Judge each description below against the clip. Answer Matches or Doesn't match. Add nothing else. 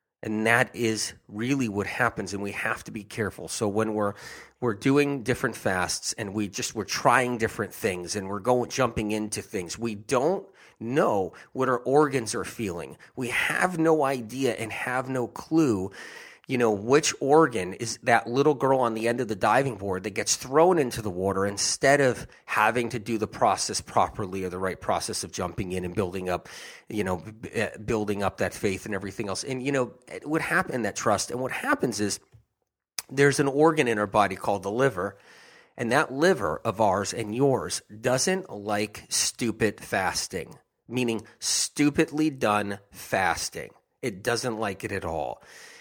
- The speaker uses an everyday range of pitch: Matches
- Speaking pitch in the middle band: Doesn't match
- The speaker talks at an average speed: Matches